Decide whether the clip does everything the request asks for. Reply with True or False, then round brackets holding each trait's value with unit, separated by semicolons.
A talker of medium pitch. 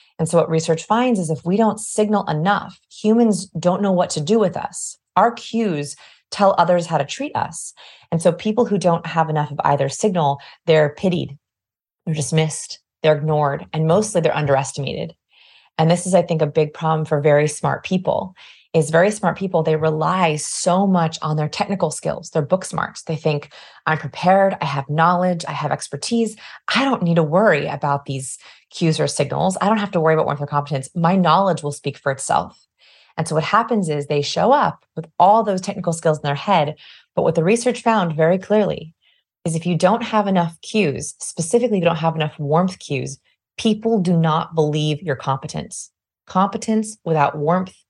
True (165 Hz)